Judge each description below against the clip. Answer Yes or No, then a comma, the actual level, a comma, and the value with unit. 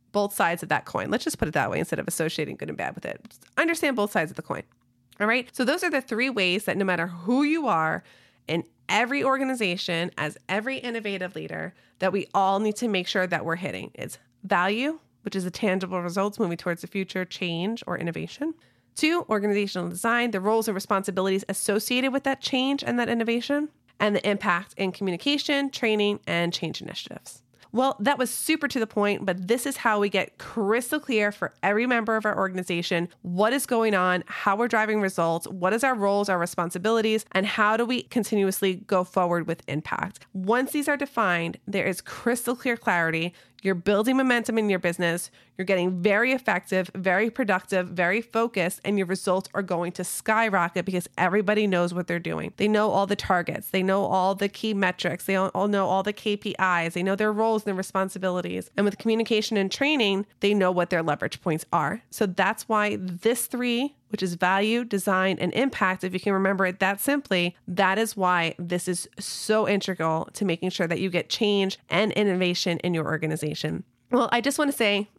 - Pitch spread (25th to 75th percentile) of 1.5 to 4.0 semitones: Yes, average, 3.7 semitones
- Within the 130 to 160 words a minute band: No, average, 200 wpm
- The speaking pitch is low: No, high, 200 Hz